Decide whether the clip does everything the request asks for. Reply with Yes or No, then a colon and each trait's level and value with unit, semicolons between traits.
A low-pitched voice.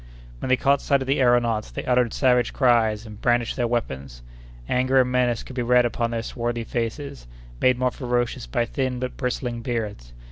Yes: low, 120 Hz